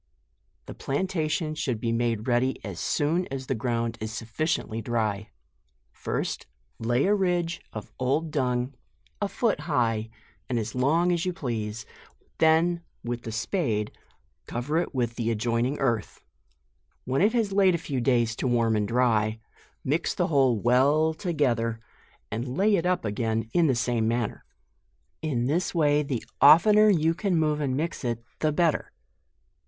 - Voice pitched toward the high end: No, low, 130 Hz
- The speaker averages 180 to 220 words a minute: No, average, 160 wpm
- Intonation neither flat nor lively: No, wide, 5.8 semitones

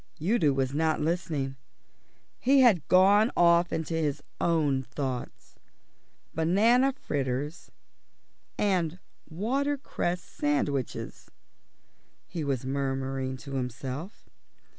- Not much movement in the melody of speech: No, average, 5.2 semitones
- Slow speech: Yes, slow, 90 wpm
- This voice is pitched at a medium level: Yes, medium, 155 Hz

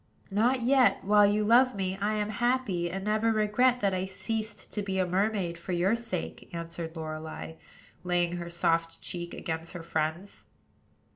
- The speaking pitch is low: No, high, 190 Hz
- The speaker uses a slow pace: No, average, 165 wpm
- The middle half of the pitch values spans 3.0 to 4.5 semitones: Yes, average, 3.9 semitones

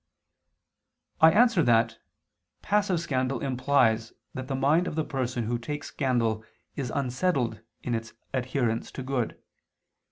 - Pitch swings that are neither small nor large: Yes, average, 3.7 semitones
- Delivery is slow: Yes, slow, 130 wpm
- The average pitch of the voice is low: Yes, low, 130 Hz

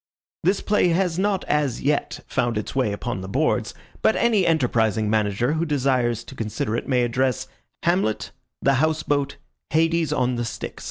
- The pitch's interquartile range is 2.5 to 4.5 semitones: No, wide, 5.6 semitones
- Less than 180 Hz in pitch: Yes, low, 135 Hz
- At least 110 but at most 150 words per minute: No, average, 170 wpm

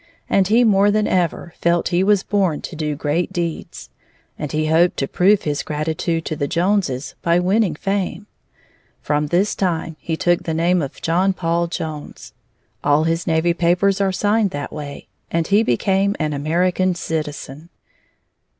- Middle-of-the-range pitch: Yes, medium, 170 Hz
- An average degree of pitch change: Yes, average, 3.5 semitones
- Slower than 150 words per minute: No, average, 165 wpm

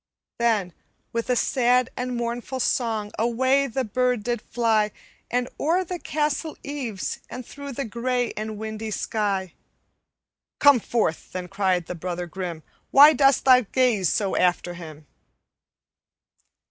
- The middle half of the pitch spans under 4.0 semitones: No, average, 4.3 semitones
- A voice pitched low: No, high, 235 Hz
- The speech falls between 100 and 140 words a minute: Yes, slow, 135 wpm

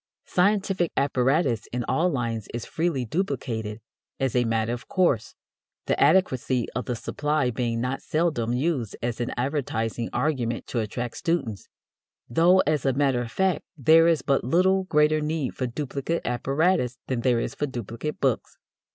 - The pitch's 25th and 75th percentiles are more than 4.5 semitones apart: Yes, average, 5.0 semitones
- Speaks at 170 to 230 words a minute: No, average, 160 wpm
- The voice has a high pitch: No, low, 130 Hz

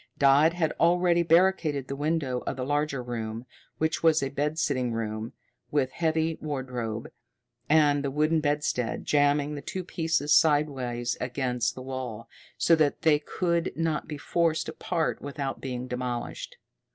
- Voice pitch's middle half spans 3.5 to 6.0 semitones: Yes, average, 3.9 semitones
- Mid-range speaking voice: Yes, medium, 145 Hz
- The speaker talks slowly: No, average, 150 wpm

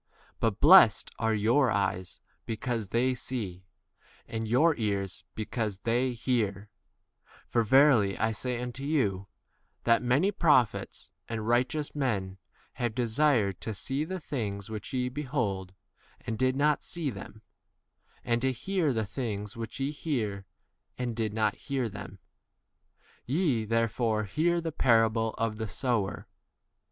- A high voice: No, low, 115 Hz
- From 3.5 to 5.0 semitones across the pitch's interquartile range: Yes, average, 3.8 semitones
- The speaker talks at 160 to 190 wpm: No, average, 145 wpm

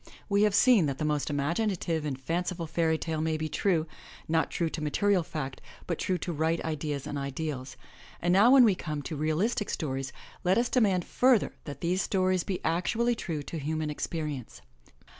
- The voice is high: No, medium, 160 Hz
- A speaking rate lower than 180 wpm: No, average, 185 wpm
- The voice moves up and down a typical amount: Yes, average, 3.8 semitones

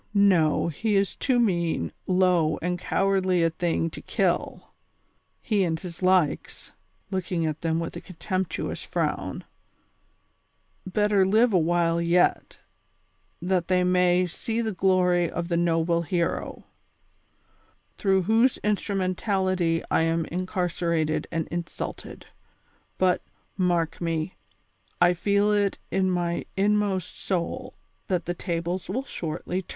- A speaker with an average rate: No, slow, 130 wpm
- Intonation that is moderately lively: No, narrow, 2.3 semitones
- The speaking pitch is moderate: Yes, medium, 180 Hz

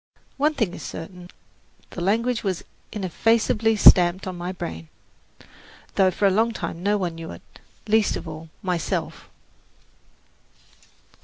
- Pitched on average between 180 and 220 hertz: Yes, high, 190 Hz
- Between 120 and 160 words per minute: Yes, slow, 135 wpm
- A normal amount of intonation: Yes, average, 4.0 semitones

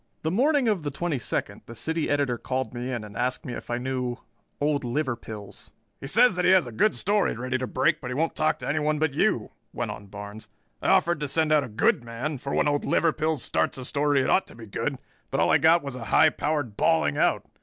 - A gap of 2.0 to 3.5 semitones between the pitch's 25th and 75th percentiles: No, average, 4.5 semitones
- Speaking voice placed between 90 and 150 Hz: Yes, medium, 140 Hz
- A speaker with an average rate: No, fast, 245 wpm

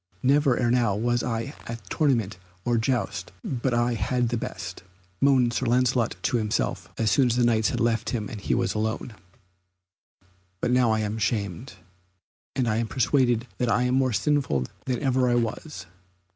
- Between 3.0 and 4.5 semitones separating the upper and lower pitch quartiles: No, narrow, 2.4 semitones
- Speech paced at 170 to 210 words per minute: Yes, average, 180 wpm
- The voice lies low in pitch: Yes, low, 120 Hz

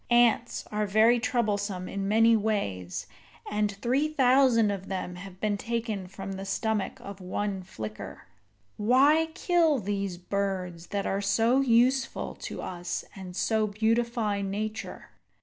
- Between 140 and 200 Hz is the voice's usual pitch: No, high, 210 Hz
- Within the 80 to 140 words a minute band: Yes, slow, 135 wpm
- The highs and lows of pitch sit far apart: No, average, 3.3 semitones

